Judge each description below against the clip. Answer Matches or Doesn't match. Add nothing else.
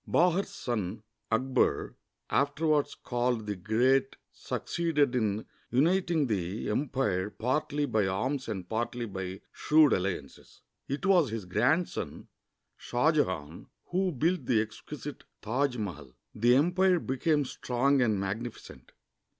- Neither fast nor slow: Doesn't match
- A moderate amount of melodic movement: Doesn't match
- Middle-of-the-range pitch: Doesn't match